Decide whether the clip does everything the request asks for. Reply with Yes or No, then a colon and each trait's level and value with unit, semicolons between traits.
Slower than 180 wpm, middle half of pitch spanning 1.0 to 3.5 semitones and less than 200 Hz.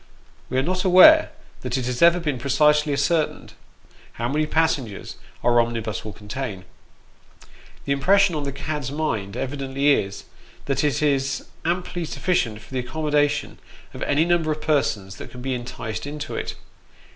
No: average, 160 wpm; average, 4.1 semitones; medium, 140 Hz